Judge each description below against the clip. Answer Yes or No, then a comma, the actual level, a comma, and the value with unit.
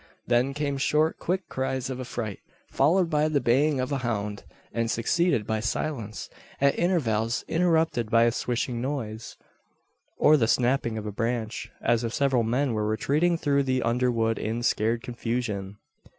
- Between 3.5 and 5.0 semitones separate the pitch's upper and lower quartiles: Yes, average, 3.8 semitones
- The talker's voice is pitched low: Yes, low, 125 Hz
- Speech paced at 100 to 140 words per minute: No, average, 160 wpm